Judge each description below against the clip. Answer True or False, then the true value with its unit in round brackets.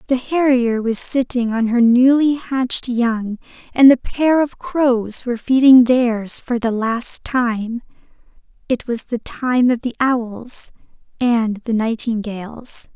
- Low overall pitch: False (240 Hz)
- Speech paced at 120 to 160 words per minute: True (140 wpm)